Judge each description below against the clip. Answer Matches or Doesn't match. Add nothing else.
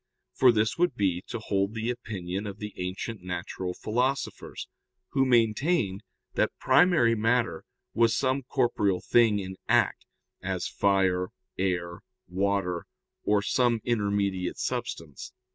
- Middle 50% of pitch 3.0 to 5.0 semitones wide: Matches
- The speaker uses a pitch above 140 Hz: Doesn't match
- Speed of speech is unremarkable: Doesn't match